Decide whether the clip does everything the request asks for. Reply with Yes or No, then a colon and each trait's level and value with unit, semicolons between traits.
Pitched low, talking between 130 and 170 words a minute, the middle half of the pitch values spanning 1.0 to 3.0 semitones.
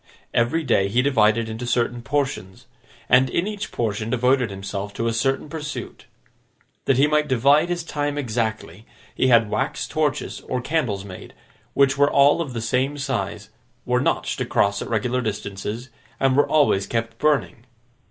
No: low, 125 Hz; average, 160 wpm; average, 4.3 semitones